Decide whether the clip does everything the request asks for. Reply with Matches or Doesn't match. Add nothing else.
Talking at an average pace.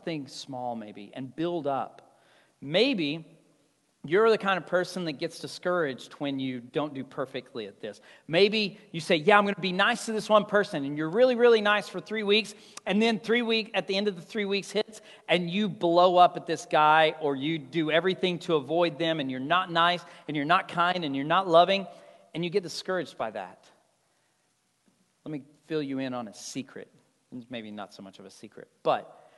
Doesn't match